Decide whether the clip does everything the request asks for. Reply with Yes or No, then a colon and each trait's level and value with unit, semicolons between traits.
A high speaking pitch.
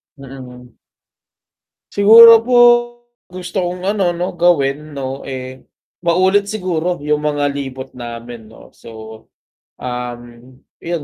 No: medium, 145 Hz